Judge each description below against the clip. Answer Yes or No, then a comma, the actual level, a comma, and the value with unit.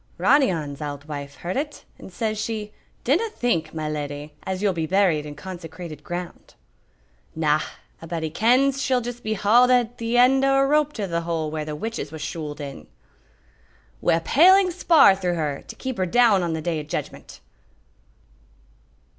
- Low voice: No, medium, 185 Hz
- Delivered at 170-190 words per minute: Yes, average, 180 wpm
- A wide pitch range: Yes, wide, 7.7 semitones